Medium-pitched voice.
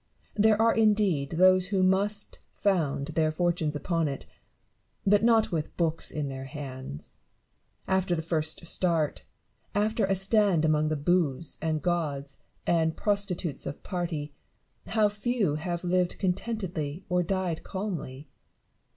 Yes: medium, 175 Hz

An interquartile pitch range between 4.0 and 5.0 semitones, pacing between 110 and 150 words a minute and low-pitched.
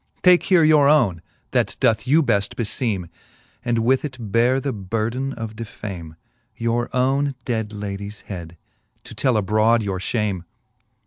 Yes: average, 4.3 semitones; average, 145 wpm; low, 115 Hz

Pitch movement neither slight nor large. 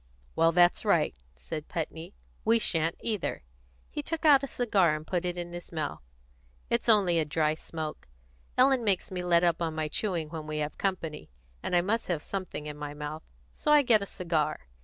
Yes: average, 4.4 semitones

